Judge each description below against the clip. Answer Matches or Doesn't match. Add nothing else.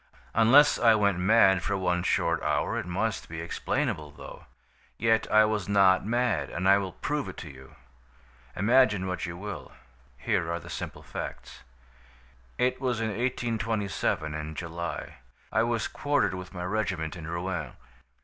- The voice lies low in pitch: Matches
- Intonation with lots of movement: Doesn't match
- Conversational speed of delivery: Matches